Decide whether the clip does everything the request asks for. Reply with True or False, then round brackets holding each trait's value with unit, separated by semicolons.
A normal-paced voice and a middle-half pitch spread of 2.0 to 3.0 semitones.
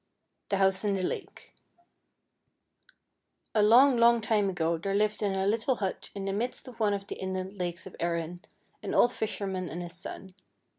True (185 wpm; 2.6 semitones)